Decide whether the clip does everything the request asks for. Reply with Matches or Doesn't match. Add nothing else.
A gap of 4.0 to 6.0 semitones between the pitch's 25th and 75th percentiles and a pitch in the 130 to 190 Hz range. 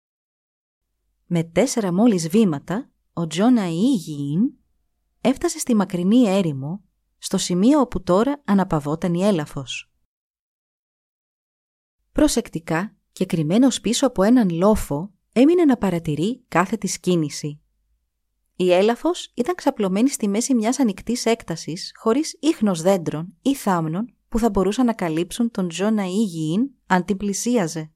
Doesn't match